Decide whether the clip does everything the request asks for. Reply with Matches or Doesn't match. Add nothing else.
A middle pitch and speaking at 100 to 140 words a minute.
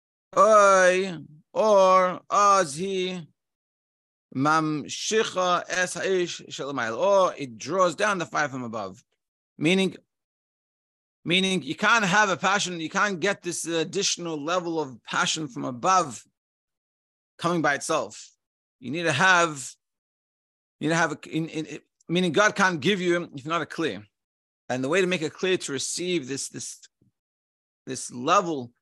Matches